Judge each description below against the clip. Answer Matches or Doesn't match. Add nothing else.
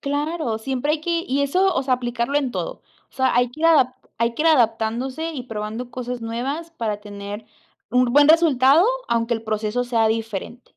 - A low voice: Doesn't match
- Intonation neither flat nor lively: Matches